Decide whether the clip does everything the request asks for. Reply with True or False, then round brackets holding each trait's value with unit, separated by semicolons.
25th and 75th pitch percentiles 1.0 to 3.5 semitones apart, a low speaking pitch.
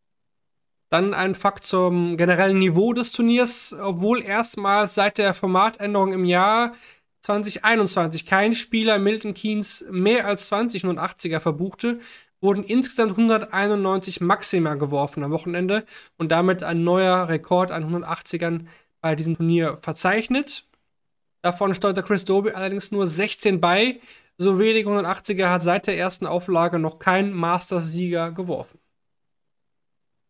False (3.0 semitones; 190 Hz)